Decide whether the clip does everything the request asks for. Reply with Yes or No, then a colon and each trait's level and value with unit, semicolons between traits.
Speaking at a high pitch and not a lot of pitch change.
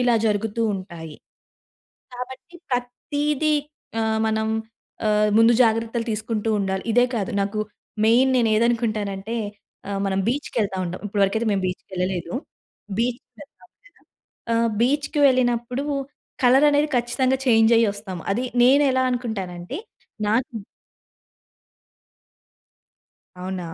No: high, 225 Hz; average, 3.7 semitones